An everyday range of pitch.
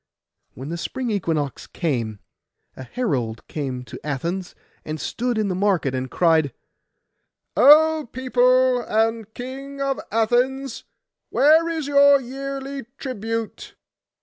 No: wide, 8.9 semitones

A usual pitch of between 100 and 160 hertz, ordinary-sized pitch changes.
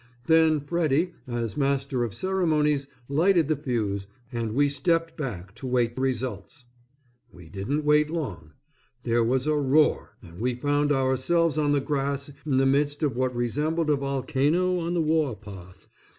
Yes: medium, 140 Hz; average, 3.9 semitones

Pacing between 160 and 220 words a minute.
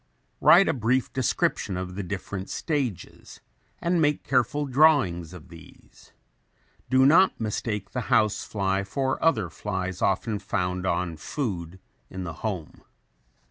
No: slow, 135 wpm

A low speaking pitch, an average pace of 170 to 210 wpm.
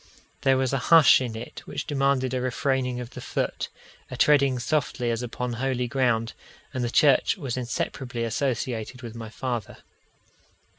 No: low, 125 Hz; average, 160 wpm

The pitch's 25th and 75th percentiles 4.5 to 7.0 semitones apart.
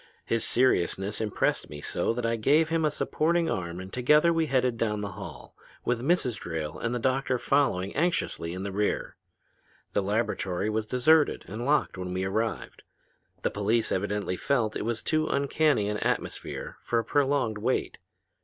Yes: wide, 5.5 semitones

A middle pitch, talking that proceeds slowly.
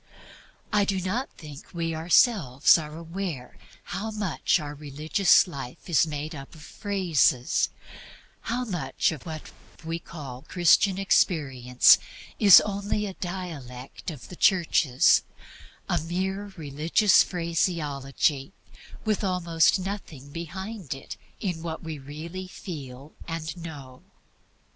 Yes: medium, 165 Hz; slow, 120 wpm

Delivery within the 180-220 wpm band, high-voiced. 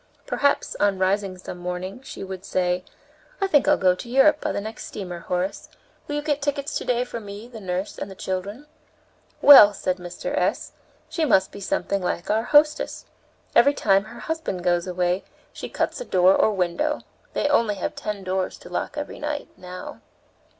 Yes: average, 185 wpm; high, 200 Hz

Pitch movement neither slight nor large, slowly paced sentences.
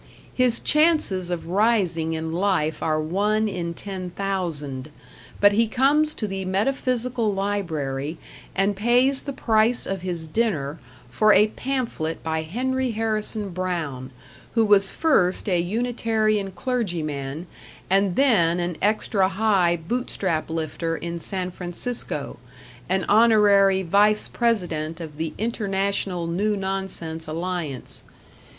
Yes: average, 4.7 semitones; slow, 120 wpm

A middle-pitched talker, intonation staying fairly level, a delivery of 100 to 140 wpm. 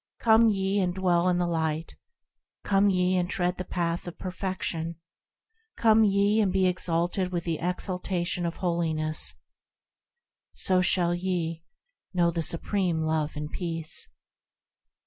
Yes: medium, 180 Hz; narrow, 2.0 semitones; slow, 135 wpm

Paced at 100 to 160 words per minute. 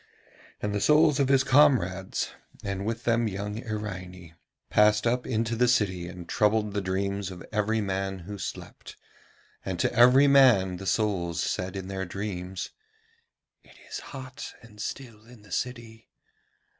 Yes: average, 155 wpm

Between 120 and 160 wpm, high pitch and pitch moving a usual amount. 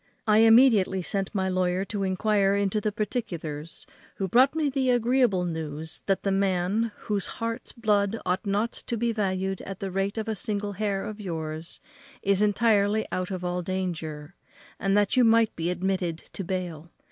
No: average, 175 wpm; high, 195 Hz; average, 3.0 semitones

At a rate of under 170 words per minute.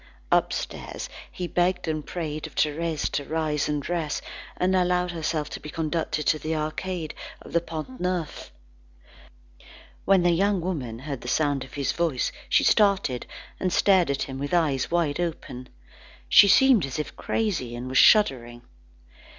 Yes: average, 160 wpm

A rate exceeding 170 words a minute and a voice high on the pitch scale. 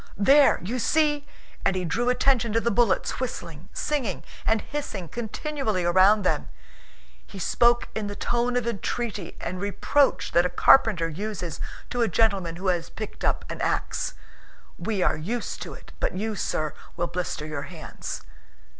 No: average, 165 wpm; high, 210 Hz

